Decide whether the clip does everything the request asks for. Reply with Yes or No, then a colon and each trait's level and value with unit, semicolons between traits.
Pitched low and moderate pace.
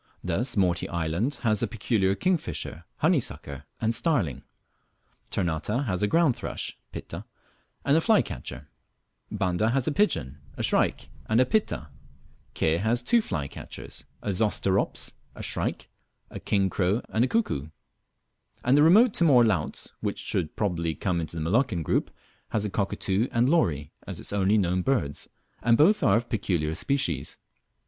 Yes: low, 105 Hz; average, 155 wpm